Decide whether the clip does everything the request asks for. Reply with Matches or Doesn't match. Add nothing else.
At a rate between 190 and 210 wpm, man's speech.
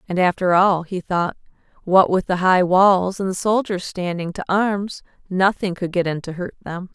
Doesn't match